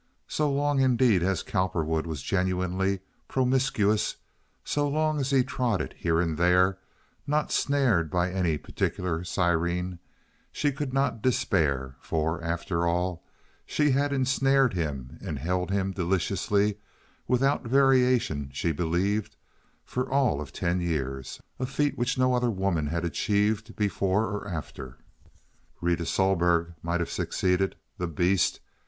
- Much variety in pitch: Yes, wide, 6.7 semitones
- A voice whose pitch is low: Yes, very low, 95 Hz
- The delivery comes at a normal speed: No, slow, 125 wpm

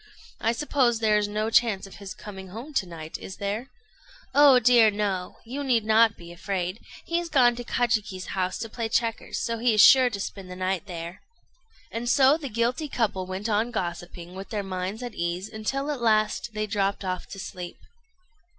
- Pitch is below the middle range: No, high, 215 Hz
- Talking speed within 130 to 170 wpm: No, average, 195 wpm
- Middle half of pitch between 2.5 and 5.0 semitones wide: Yes, average, 4.1 semitones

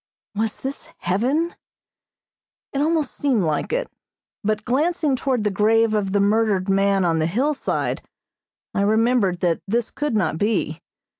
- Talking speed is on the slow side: No, average, 145 wpm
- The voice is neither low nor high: No, high, 215 Hz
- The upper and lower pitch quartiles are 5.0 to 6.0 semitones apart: Yes, average, 5.3 semitones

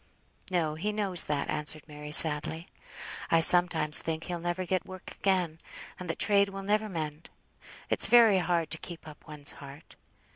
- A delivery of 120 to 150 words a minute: No, average, 170 wpm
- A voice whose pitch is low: No, medium, 170 Hz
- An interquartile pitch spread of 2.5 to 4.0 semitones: Yes, average, 3.4 semitones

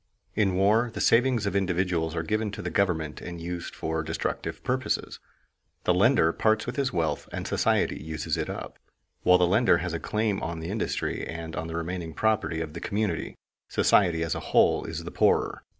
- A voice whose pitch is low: Yes, very low, 90 Hz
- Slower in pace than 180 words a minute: No, average, 195 wpm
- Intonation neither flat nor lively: Yes, average, 4.6 semitones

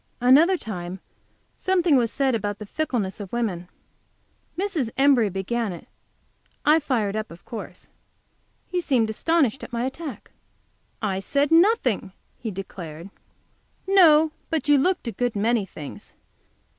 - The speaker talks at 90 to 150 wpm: Yes, slow, 135 wpm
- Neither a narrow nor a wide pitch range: No, wide, 6.9 semitones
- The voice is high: Yes, high, 240 Hz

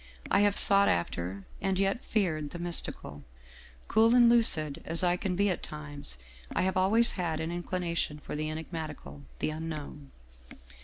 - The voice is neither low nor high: Yes, medium, 170 Hz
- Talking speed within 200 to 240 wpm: No, average, 160 wpm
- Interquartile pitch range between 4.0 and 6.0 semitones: Yes, average, 4.3 semitones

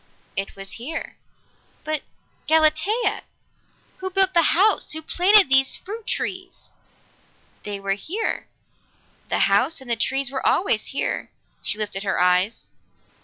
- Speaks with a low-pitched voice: No, very high, 305 Hz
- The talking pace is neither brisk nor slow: No, slow, 125 wpm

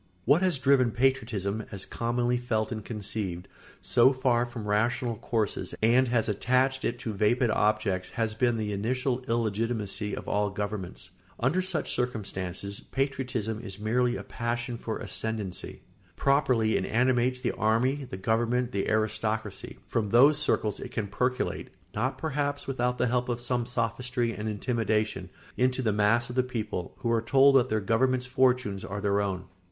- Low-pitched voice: Yes, low, 115 Hz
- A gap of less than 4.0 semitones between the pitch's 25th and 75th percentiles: Yes, average, 3.0 semitones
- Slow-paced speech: No, average, 165 wpm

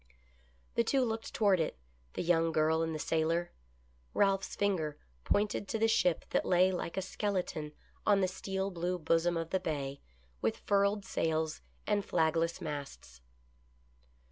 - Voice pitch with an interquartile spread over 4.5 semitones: No, average, 3.7 semitones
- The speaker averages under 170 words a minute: Yes, average, 155 wpm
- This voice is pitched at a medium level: Yes, medium, 175 Hz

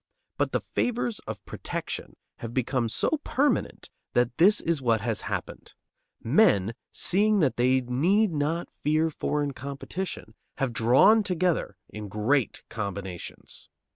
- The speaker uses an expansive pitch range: Yes, wide, 7.7 semitones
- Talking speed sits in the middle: No, slow, 130 wpm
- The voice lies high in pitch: No, medium, 140 Hz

